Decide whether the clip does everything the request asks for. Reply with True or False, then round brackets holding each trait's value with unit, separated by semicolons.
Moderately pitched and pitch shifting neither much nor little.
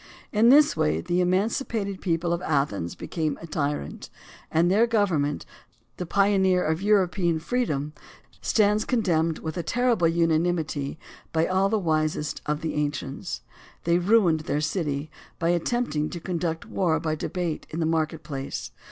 True (170 Hz; 3.9 semitones)